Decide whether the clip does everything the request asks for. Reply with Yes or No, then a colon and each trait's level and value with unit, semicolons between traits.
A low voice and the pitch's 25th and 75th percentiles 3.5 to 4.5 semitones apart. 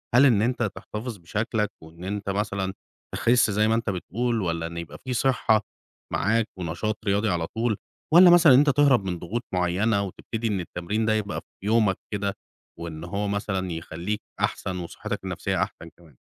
Yes: low, 105 Hz; average, 4.1 semitones